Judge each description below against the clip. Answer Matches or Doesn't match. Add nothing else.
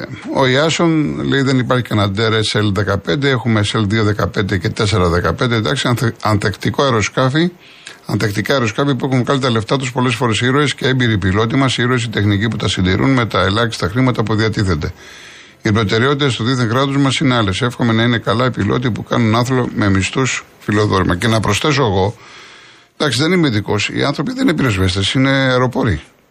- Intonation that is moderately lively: Matches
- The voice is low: Matches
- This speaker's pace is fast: Matches